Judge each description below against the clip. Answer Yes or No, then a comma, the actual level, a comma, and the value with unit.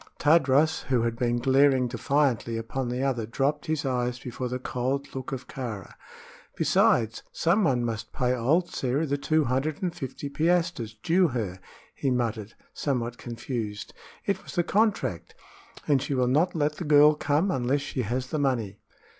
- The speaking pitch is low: Yes, low, 130 Hz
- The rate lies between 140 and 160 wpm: No, average, 170 wpm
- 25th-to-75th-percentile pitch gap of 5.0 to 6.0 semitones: No, average, 3.7 semitones